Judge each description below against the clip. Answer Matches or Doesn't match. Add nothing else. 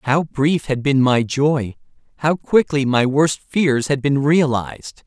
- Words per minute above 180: Doesn't match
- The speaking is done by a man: Matches